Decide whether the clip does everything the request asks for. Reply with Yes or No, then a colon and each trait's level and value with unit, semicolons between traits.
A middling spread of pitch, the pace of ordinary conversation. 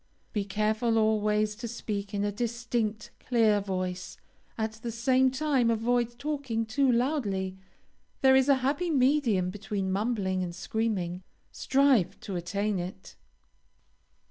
No: average, 3.7 semitones; slow, 130 wpm